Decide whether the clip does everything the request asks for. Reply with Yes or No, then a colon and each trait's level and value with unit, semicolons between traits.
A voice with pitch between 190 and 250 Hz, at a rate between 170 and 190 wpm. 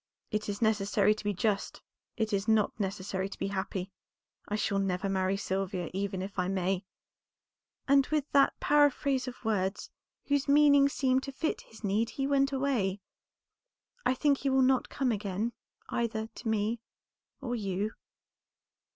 No: high, 215 Hz; average, 160 wpm